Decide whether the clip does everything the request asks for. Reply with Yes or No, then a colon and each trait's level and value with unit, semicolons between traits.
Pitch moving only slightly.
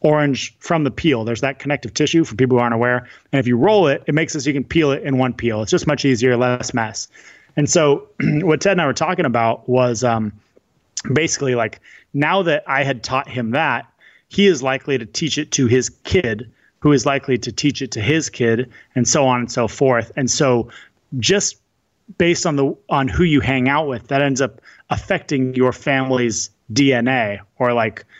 No: average, 3.6 semitones